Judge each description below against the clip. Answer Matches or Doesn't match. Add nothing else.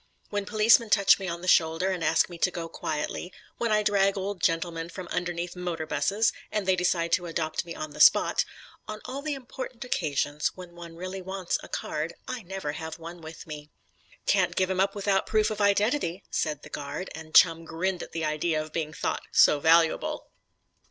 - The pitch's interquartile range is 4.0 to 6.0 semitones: Doesn't match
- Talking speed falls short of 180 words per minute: Doesn't match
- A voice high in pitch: Doesn't match